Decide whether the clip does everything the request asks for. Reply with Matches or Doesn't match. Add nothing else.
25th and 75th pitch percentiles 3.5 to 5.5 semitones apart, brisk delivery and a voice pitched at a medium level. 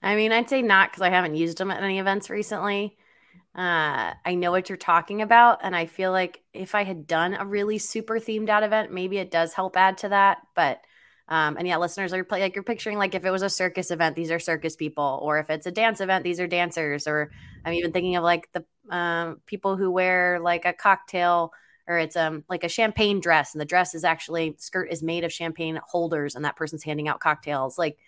Doesn't match